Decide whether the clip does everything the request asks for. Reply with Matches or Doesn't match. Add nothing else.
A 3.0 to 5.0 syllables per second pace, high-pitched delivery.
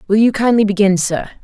Doesn't match